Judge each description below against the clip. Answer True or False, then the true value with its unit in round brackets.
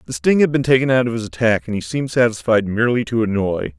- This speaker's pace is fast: True (255 wpm)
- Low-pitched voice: True (115 Hz)